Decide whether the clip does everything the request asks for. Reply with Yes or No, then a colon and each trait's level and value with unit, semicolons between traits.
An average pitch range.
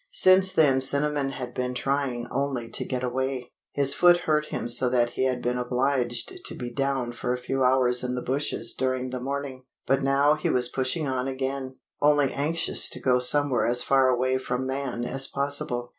No: narrow, 1.9 semitones